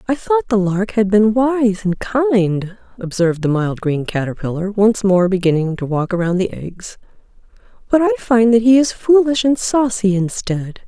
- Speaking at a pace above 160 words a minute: Yes, average, 175 wpm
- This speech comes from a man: No, female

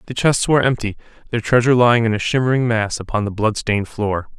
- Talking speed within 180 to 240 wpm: Yes, fast, 205 wpm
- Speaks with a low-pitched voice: Yes, low, 115 Hz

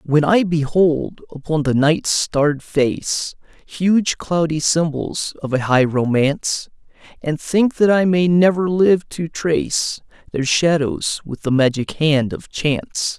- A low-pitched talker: No, medium, 155 Hz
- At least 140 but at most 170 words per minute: Yes, average, 145 wpm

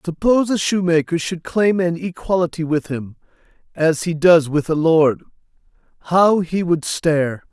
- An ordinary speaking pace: Yes, average, 150 wpm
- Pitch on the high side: No, medium, 165 Hz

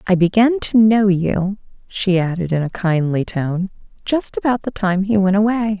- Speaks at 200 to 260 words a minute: No, average, 185 wpm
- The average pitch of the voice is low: No, high, 195 Hz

